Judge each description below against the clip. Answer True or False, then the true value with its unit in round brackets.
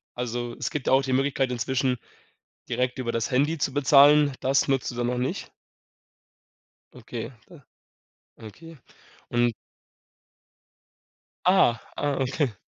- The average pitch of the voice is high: False (130 Hz)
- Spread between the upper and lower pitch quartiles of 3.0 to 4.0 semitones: False (2.6 semitones)